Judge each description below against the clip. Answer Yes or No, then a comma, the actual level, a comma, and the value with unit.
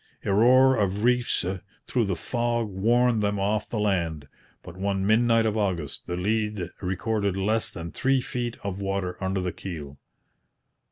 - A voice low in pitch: Yes, low, 100 Hz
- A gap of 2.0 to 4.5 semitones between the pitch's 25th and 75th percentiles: Yes, average, 3.5 semitones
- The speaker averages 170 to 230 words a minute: No, average, 160 wpm